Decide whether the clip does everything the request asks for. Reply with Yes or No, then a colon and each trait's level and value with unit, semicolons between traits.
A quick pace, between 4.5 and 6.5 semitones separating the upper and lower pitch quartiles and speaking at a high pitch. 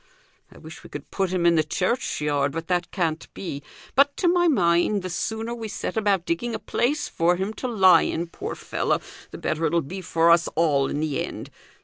No: fast, 215 wpm; average, 5.1 semitones; medium, 175 Hz